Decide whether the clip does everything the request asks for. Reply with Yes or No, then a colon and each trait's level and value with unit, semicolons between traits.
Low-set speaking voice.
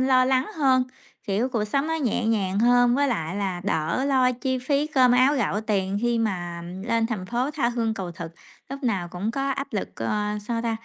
No: high, 235 Hz